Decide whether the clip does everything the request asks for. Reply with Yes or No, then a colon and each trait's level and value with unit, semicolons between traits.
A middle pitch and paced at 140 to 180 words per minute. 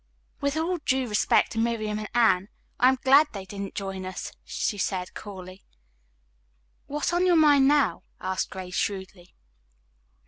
No: high, 215 Hz; average, 160 wpm